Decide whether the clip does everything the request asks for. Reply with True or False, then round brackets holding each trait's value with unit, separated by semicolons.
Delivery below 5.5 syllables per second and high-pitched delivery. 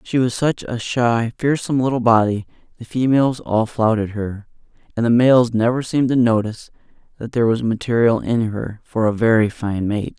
False (5.3 syllables/s; 115 Hz)